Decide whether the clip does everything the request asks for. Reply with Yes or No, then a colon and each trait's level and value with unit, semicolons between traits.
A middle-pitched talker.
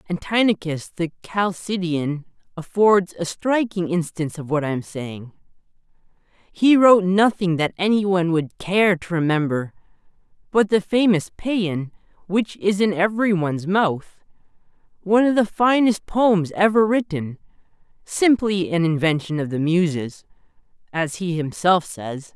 Yes: medium, 180 Hz